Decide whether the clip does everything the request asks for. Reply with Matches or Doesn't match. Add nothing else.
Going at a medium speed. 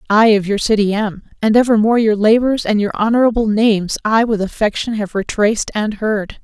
Matches